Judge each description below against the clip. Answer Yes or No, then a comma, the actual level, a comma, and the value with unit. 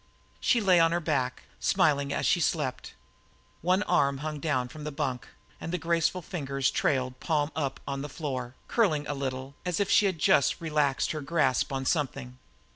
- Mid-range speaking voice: Yes, medium, 150 Hz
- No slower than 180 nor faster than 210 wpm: Yes, average, 185 wpm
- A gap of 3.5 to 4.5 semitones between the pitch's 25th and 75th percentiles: Yes, average, 3.8 semitones